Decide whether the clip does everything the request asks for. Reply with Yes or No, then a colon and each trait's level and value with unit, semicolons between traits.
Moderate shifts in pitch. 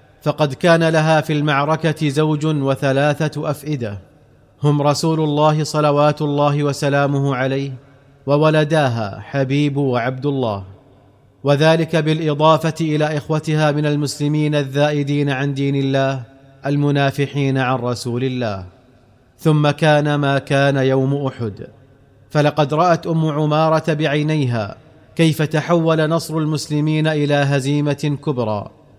No: narrow, 2.1 semitones